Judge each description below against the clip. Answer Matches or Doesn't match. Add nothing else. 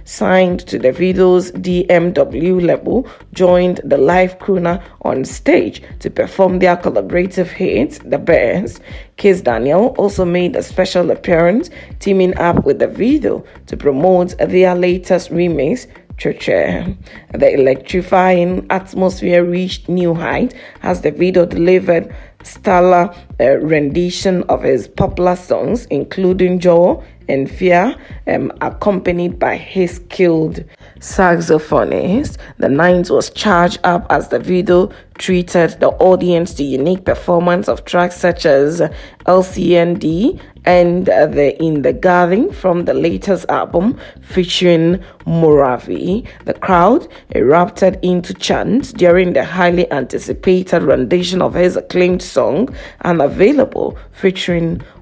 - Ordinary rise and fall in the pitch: Doesn't match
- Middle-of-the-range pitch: Matches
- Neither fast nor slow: Doesn't match